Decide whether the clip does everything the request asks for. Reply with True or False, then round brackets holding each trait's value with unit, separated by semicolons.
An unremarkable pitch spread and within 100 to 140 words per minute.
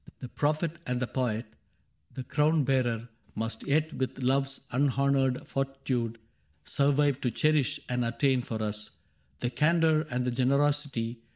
True (3.0 semitones; 135 wpm)